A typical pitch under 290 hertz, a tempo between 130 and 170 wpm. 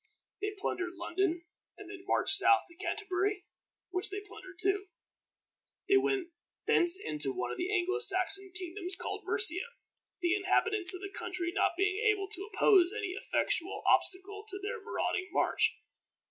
No: very high, 380 Hz; average, 155 wpm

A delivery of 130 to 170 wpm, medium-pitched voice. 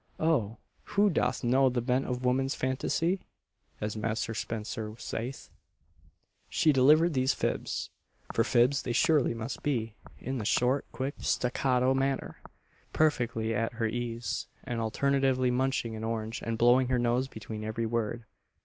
No: average, 145 wpm; low, 125 Hz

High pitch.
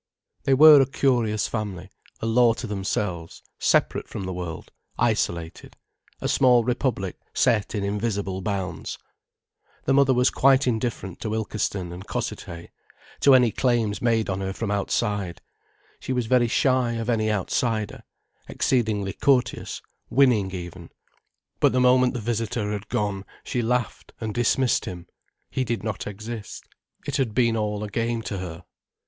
No: low, 110 Hz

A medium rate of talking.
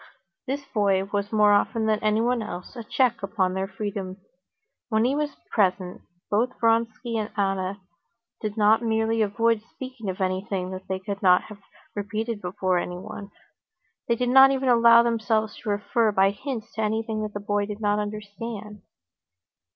Yes: average, 160 wpm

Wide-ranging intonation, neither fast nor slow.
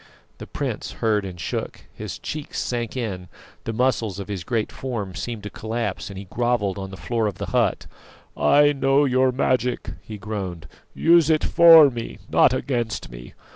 No: average, 4.6 semitones; average, 175 wpm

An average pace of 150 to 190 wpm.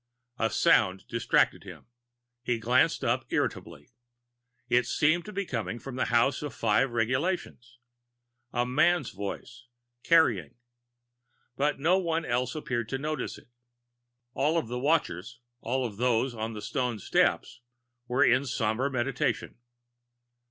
No: slow, 135 wpm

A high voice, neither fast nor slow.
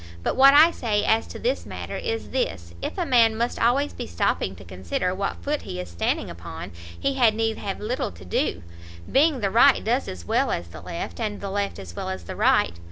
No: high, 205 Hz; fast, 230 wpm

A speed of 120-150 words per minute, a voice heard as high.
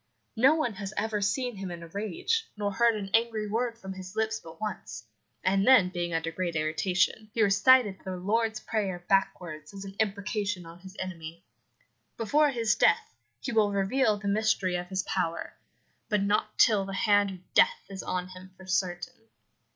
No: average, 180 wpm; high, 200 Hz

